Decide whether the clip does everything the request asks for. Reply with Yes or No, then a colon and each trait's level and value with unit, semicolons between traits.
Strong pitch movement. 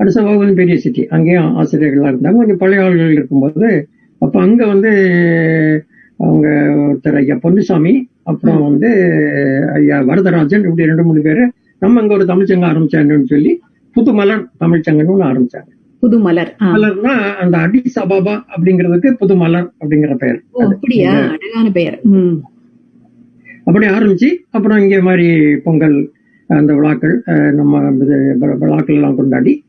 Yes: wide, 5.9 semitones